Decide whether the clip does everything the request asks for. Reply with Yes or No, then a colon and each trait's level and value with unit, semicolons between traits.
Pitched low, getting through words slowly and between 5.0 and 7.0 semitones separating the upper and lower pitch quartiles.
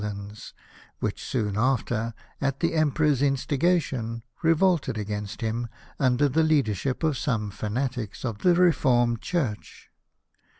Yes: low, 125 Hz; slow, 125 wpm; wide, 5.5 semitones